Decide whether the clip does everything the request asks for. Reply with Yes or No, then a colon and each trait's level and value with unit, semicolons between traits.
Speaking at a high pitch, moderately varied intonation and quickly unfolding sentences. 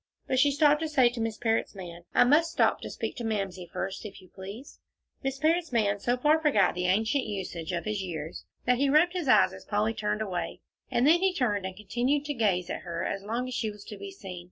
No: high, 220 Hz; wide, 6.5 semitones; fast, 245 wpm